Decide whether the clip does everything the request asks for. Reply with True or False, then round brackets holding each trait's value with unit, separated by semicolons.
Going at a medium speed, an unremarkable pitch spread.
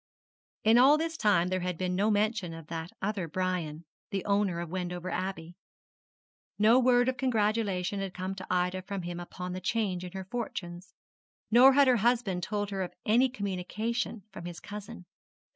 True (175 wpm; 3.6 semitones)